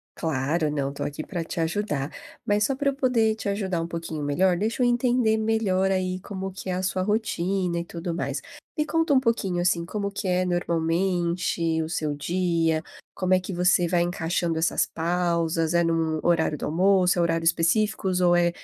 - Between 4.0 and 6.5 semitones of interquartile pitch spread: No, average, 3.1 semitones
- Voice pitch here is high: No, medium, 180 Hz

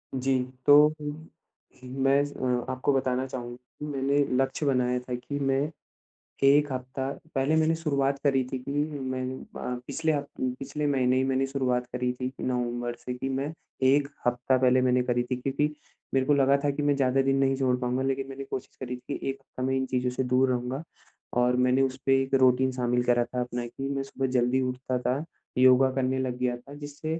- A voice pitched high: No, low, 130 Hz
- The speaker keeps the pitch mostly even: Yes, narrow, 1.5 semitones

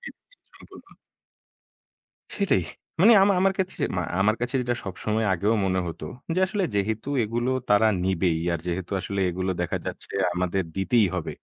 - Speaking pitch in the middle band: No, low, 105 Hz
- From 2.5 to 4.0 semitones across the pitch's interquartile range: No, average, 5.0 semitones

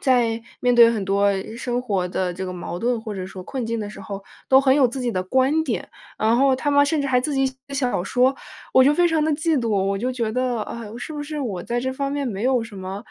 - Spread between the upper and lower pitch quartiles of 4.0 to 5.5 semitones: Yes, average, 4.6 semitones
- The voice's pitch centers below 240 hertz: No, high, 245 Hz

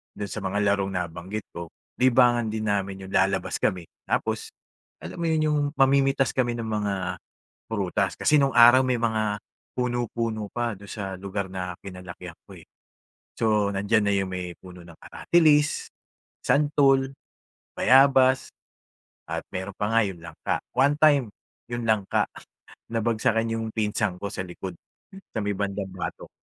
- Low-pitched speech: Yes, low, 105 Hz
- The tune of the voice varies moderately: Yes, average, 4.1 semitones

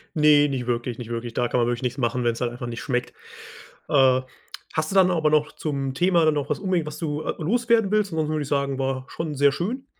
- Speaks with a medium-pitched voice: Yes, medium, 145 Hz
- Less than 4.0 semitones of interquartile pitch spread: No, average, 4.5 semitones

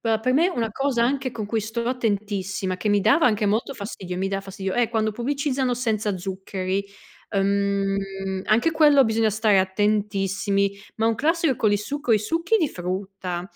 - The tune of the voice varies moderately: Yes, average, 3.8 semitones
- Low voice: No, high, 215 Hz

